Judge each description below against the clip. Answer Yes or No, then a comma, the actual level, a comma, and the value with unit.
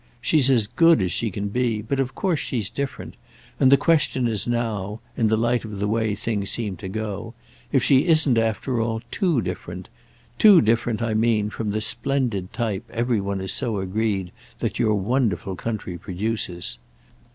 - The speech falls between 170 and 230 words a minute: Yes, average, 175 wpm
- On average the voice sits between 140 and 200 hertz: No, low, 115 Hz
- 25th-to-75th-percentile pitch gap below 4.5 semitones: Yes, average, 3.2 semitones